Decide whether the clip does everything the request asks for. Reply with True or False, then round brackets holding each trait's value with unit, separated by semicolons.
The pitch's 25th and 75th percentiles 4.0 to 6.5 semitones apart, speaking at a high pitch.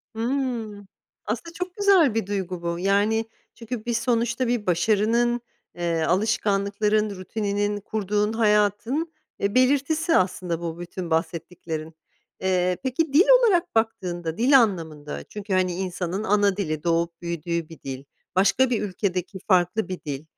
True (4.8 semitones; 205 Hz)